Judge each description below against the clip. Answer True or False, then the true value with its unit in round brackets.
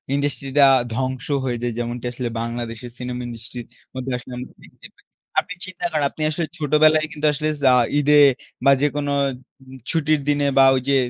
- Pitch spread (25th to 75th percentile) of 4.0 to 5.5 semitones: False (3.0 semitones)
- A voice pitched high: False (135 Hz)